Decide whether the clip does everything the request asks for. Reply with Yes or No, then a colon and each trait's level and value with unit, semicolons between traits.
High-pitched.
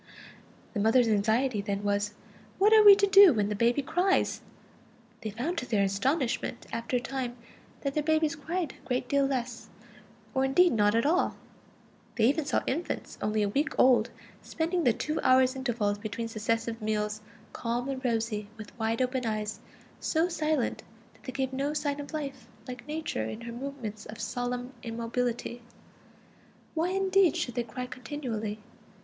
Yes: very high, 250 Hz